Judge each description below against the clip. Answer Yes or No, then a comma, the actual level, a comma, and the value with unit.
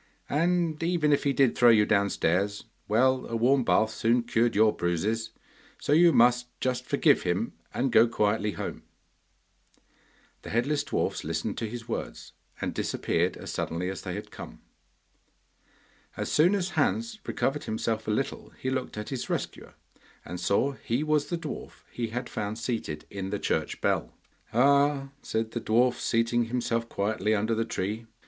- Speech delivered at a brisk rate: No, average, 165 wpm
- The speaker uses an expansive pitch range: No, average, 4.1 semitones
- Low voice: Yes, low, 115 Hz